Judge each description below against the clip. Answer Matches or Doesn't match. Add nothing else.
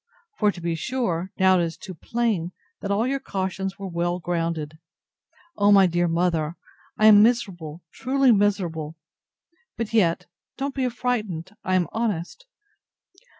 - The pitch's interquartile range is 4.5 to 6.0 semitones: Matches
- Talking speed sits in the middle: Matches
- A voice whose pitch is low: Doesn't match